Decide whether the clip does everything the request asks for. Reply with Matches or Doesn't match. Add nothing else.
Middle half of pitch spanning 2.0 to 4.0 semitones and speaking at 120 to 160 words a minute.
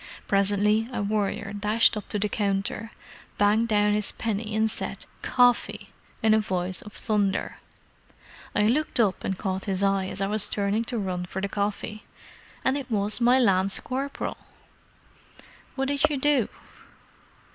Matches